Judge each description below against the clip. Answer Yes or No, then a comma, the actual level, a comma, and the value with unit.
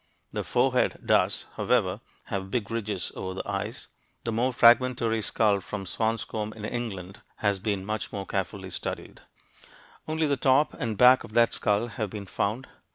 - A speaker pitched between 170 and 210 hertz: No, low, 110 Hz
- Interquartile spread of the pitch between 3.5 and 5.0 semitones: No, average, 3.0 semitones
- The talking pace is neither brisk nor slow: Yes, average, 170 wpm